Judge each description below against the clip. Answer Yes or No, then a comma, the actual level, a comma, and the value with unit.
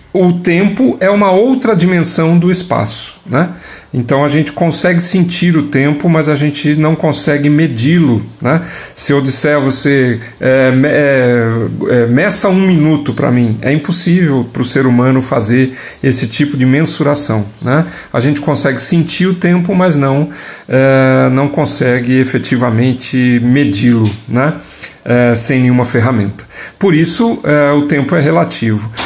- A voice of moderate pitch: Yes, medium, 145 Hz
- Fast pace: No, average, 155 wpm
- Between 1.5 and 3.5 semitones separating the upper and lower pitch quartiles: No, average, 4.3 semitones